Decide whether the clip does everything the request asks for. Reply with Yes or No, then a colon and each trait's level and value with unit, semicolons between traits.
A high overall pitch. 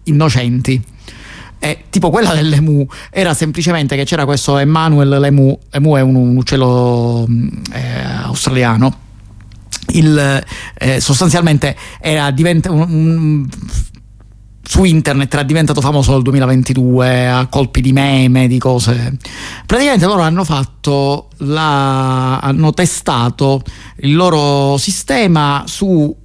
No: medium, 140 Hz